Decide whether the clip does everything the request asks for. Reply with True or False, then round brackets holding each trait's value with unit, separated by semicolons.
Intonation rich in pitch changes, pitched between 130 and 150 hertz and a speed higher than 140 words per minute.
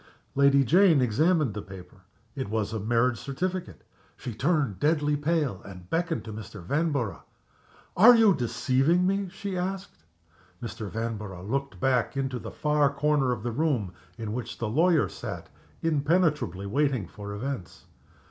True (6.5 semitones; 135 Hz; 150 wpm)